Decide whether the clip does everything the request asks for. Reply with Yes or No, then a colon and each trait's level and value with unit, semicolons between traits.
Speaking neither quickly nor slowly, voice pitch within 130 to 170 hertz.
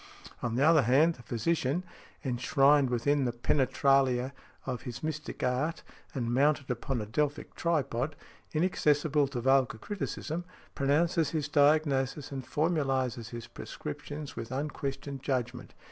No: slow, 130 wpm; medium, 140 Hz